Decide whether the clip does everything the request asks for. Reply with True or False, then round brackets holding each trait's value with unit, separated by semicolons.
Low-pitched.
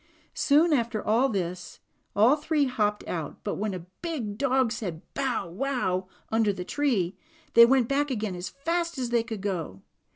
False (230 Hz)